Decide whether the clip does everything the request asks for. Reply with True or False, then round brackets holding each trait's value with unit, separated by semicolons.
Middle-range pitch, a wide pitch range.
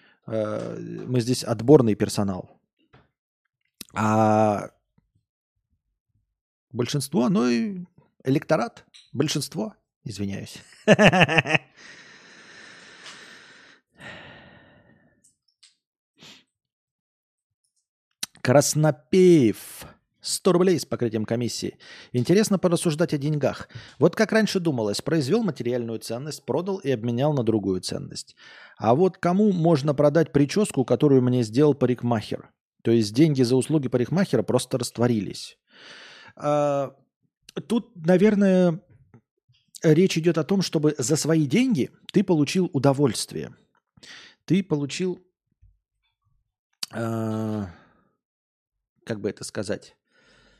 True (145 Hz; 6.9 semitones)